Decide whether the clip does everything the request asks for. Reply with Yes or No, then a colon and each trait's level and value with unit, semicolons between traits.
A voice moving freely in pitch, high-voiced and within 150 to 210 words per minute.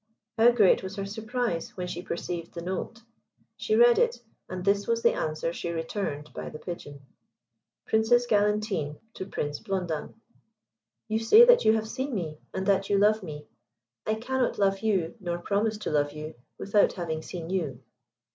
No: average, 4.7 semitones; high, 195 Hz; average, 175 wpm